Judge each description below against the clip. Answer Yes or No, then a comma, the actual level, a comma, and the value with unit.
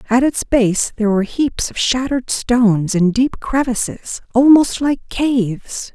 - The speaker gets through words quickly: No, average, 150 wpm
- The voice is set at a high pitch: Yes, high, 240 Hz